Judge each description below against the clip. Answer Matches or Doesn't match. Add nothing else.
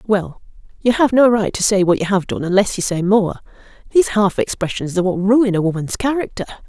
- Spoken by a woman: Matches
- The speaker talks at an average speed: Doesn't match